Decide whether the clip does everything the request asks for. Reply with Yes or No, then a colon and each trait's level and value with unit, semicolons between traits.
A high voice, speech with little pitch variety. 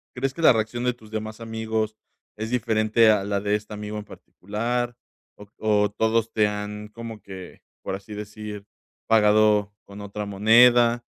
No: low, 110 Hz; narrow, 1.6 semitones